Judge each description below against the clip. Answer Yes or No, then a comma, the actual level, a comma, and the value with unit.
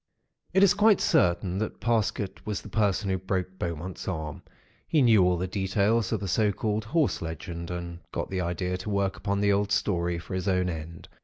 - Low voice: Yes, very low, 95 Hz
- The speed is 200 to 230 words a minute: Yes, fast, 205 wpm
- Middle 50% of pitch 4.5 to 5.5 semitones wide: No, average, 3.0 semitones